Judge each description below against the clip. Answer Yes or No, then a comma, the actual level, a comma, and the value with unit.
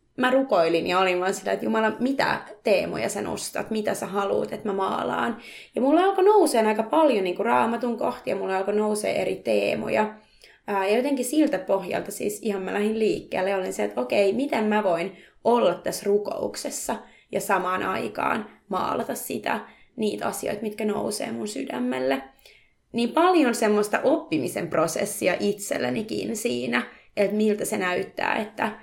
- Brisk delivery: Yes, fast, 160 wpm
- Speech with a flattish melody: No, average, 3.6 semitones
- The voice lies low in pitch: No, high, 210 Hz